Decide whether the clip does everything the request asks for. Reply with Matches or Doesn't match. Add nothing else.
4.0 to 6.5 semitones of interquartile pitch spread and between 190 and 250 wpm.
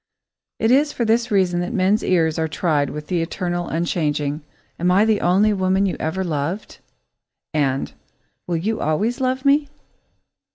Doesn't match